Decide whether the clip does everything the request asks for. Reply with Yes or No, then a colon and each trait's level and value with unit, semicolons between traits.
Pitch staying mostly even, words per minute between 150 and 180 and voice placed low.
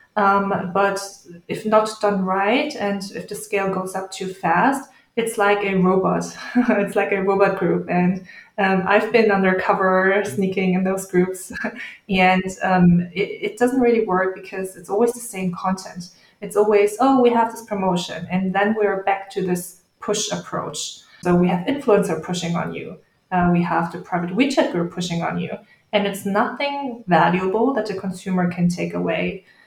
No: narrow, 2.3 semitones; average, 175 wpm; high, 195 Hz